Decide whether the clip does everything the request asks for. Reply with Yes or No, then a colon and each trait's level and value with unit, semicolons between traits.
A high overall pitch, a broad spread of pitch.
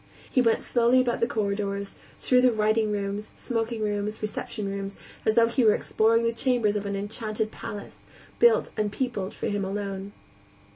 No: high, 215 Hz; narrow, 2.4 semitones